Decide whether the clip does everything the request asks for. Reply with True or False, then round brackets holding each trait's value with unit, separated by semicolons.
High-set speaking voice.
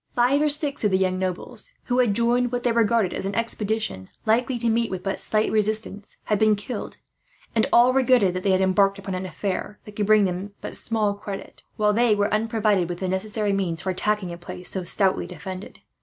True (210 Hz)